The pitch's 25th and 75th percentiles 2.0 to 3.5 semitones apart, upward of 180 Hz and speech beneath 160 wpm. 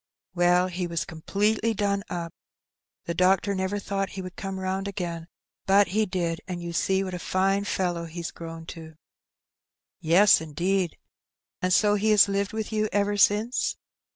No: average, 2.7 semitones; high, 190 Hz; average, 170 wpm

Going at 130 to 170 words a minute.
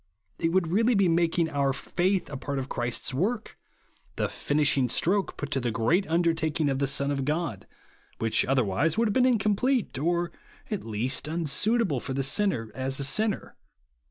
No: average, 185 wpm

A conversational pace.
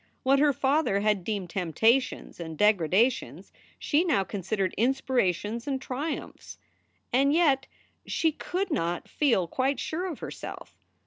No: slow, 130 wpm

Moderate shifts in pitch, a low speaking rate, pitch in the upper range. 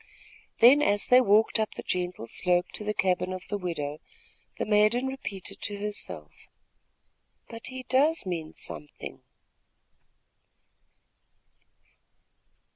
Yes: average, 4.4 semitones; slow, 115 wpm; high, 205 Hz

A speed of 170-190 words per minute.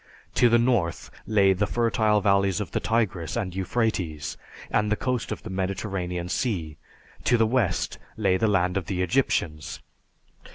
No: average, 160 wpm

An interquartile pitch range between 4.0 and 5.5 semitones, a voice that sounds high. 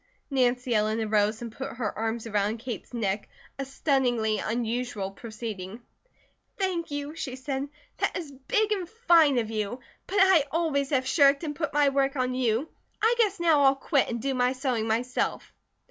Yes: average, 4.5 semitones; very high, 260 Hz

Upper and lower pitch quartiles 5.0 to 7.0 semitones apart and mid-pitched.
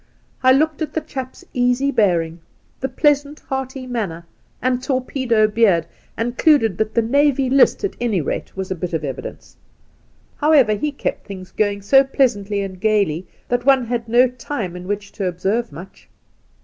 No: average, 5.3 semitones; high, 235 Hz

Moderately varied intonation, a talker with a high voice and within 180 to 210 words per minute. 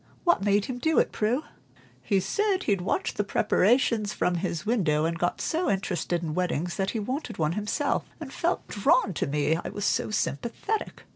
No: wide, 5.9 semitones; high, 200 Hz; average, 190 wpm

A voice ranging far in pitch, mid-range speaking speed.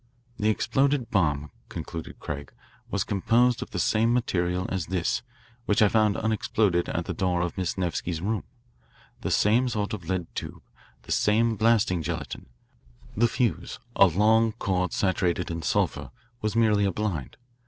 No: average, 4.1 semitones; average, 155 wpm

